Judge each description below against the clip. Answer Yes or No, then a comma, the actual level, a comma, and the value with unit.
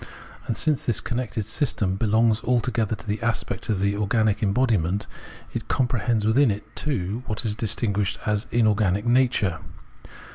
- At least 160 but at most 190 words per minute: No, average, 145 wpm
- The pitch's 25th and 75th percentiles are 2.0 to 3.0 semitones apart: Yes, narrow, 2.6 semitones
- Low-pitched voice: Yes, low, 110 Hz